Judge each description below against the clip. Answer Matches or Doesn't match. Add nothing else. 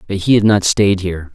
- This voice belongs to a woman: Doesn't match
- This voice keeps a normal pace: Doesn't match